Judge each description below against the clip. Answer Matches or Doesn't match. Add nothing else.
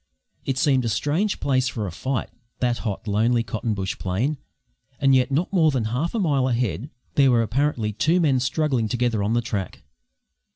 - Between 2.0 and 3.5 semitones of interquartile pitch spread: Doesn't match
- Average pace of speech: Matches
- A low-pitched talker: Matches